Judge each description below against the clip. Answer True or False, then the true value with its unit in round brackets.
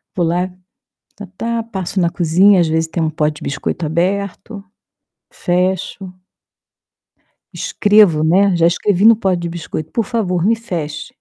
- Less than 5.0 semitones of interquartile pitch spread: True (3.2 semitones)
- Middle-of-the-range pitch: True (180 Hz)